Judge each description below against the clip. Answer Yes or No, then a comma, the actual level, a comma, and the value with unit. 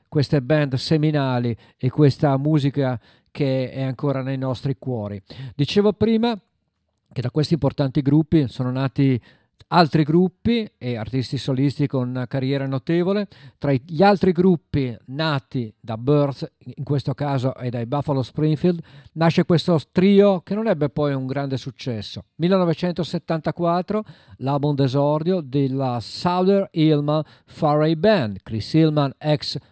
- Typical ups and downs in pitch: Yes, average, 3.8 semitones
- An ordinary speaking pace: Yes, average, 130 wpm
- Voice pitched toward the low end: No, medium, 145 Hz